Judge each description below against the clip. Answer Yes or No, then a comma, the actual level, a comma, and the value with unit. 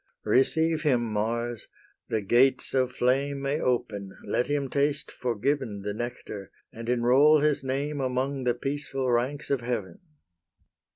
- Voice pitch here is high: No, low, 130 Hz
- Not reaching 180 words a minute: Yes, slow, 135 wpm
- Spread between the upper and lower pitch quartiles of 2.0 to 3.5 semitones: Yes, average, 2.9 semitones